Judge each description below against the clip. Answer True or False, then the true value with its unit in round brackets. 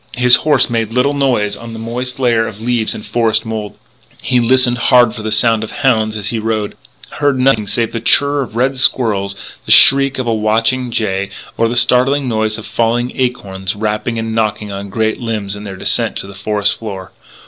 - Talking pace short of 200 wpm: False (205 wpm)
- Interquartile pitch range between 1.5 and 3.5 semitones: True (2.6 semitones)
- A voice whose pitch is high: False (115 Hz)